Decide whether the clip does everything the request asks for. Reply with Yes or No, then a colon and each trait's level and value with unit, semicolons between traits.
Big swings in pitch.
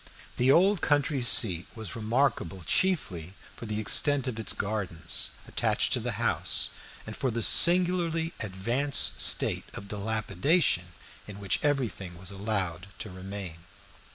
Yes: wide, 6.6 semitones